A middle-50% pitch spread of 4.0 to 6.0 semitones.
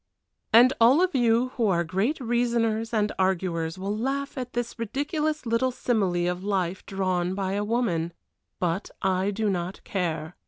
Yes: average, 4.7 semitones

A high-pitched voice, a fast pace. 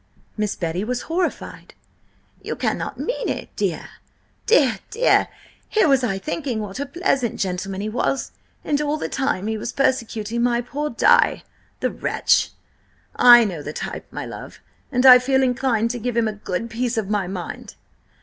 No: high, 240 Hz; average, 170 wpm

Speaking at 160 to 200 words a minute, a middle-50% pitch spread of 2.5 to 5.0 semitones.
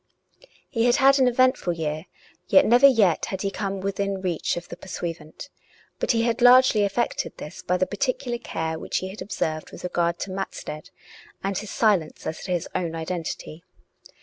No: average, 180 wpm; wide, 5.6 semitones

